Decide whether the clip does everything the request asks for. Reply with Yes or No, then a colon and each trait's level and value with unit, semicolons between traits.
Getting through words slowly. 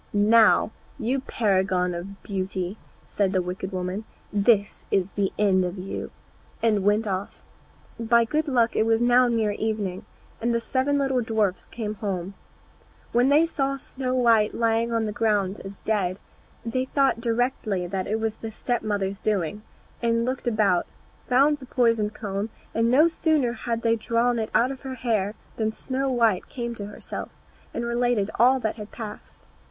No: average, 170 wpm